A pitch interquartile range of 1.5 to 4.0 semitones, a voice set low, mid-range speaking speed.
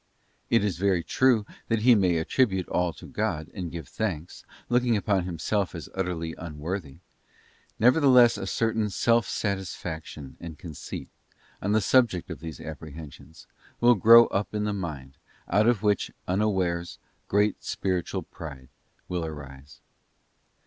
No: average, 4.7 semitones; very low, 95 Hz; average, 145 wpm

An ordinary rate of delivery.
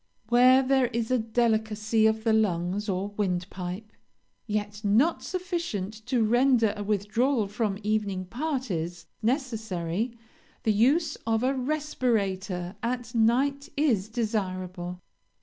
No: slow, 115 wpm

